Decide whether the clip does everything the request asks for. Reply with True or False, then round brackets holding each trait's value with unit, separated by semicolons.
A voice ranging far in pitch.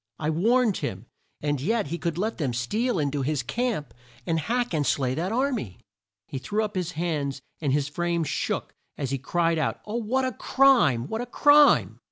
True (8.0 semitones)